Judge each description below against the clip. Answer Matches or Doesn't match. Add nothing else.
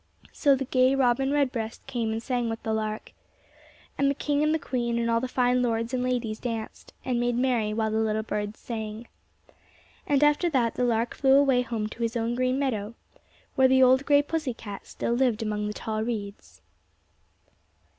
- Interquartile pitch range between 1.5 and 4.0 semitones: Matches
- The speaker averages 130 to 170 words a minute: Doesn't match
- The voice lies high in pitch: Matches